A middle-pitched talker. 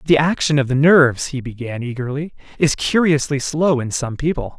Yes: medium, 145 Hz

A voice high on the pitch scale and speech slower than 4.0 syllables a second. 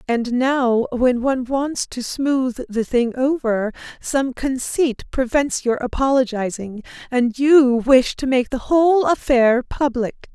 Yes: very high, 255 Hz; 3.8 syllables/s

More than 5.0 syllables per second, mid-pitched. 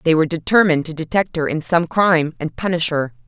Yes: 6.3 syllables/s; medium, 165 Hz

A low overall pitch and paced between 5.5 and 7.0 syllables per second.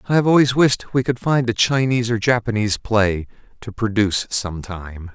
Yes: low, 115 Hz; 5.6 syllables/s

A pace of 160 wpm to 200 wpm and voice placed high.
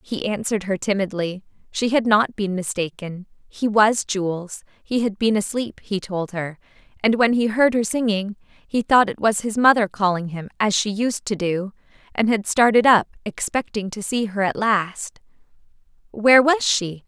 Yes: average, 180 wpm; high, 210 Hz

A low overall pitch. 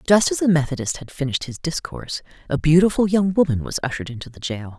No: medium, 155 Hz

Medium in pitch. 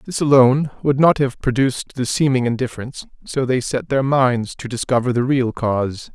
No: low, 130 Hz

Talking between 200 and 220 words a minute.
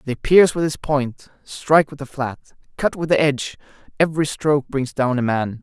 Yes: fast, 205 wpm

